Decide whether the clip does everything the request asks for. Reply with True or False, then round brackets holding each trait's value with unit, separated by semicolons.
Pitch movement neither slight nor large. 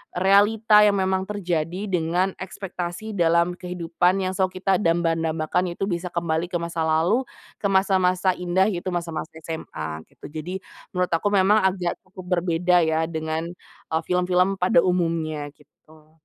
False (2.3 semitones)